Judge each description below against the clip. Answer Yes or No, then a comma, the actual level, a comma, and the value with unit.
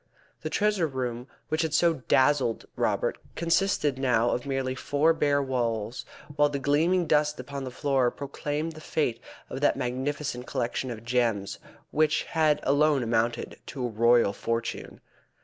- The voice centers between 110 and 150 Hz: Yes, low, 135 Hz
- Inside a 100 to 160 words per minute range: Yes, average, 150 wpm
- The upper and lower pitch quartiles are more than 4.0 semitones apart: No, average, 3.7 semitones